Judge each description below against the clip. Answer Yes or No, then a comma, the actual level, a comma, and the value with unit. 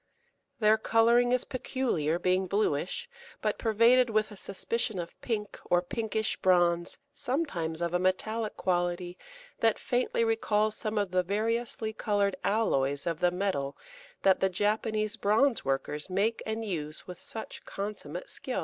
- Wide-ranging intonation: No, average, 4.1 semitones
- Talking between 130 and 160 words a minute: Yes, average, 140 wpm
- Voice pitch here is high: Yes, high, 210 Hz